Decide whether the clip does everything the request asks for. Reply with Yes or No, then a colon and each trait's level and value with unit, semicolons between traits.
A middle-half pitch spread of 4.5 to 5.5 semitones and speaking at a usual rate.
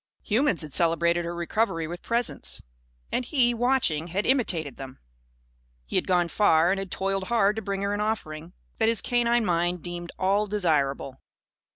Yes: average, 4.8 semitones; average, 170 wpm